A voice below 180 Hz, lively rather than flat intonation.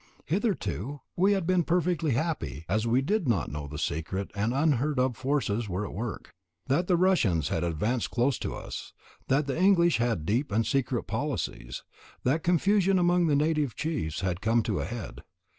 Yes: low, 135 Hz; wide, 8.1 semitones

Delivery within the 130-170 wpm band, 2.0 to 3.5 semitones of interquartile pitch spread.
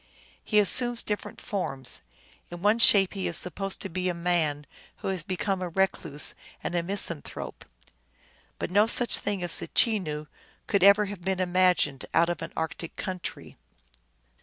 Yes: average, 160 wpm; average, 2.9 semitones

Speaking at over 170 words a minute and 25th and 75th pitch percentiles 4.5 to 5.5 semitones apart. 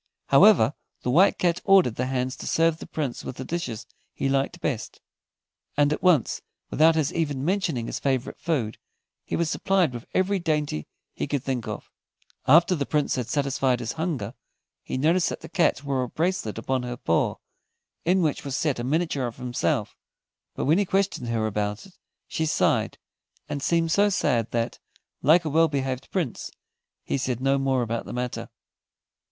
Yes: average, 180 wpm; average, 4.8 semitones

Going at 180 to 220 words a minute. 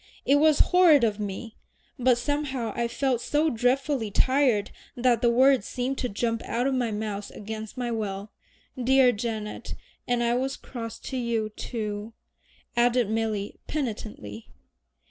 No: average, 145 wpm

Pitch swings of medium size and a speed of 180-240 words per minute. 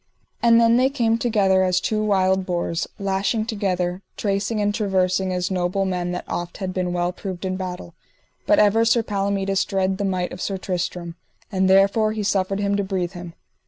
No: narrow, 2.2 semitones; average, 190 wpm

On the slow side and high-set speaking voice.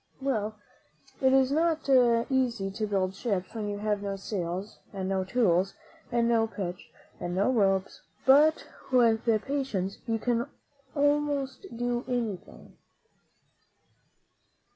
Yes: slow, 120 wpm; high, 225 Hz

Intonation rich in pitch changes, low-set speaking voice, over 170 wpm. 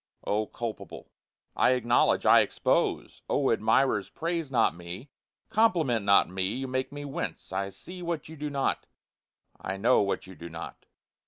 No: wide, 6.5 semitones; low, 125 Hz; average, 160 wpm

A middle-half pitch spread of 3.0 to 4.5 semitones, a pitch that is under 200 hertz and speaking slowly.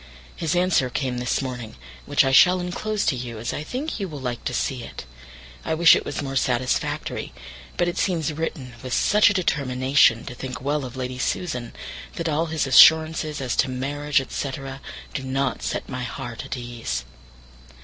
No: average, 4.2 semitones; low, 135 Hz; average, 180 wpm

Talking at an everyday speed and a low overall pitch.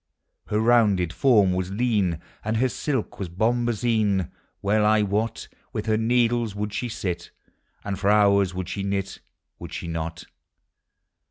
Yes: average, 150 wpm; low, 105 Hz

